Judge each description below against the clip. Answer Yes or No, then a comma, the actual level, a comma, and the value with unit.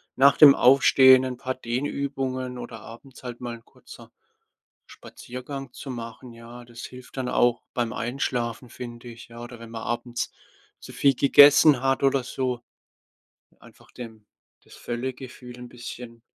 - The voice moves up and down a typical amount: No, narrow, 1.8 semitones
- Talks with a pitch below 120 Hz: No, low, 125 Hz